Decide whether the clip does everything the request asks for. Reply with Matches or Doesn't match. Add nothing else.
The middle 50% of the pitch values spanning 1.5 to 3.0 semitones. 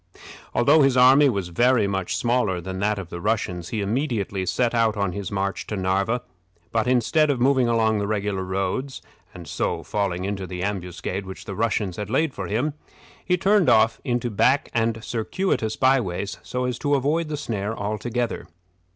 Doesn't match